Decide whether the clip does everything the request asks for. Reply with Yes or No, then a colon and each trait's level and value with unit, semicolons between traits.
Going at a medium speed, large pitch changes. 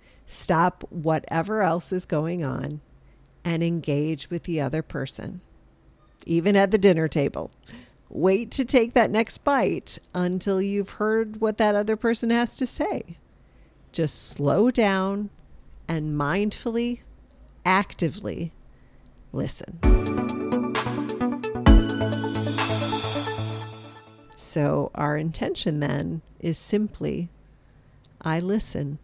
No: slow, 100 wpm; wide, 6.7 semitones